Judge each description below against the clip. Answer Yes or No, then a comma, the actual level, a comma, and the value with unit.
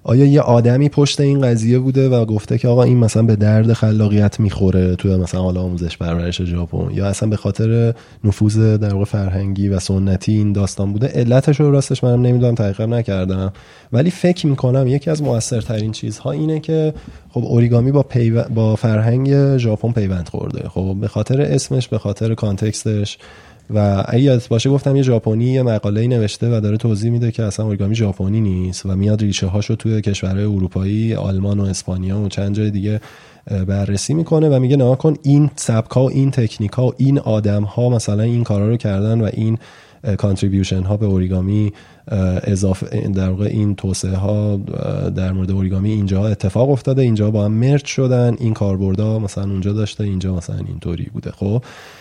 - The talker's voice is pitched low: Yes, low, 110 Hz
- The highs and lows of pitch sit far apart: No, average, 3.6 semitones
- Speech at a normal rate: No, fast, 180 wpm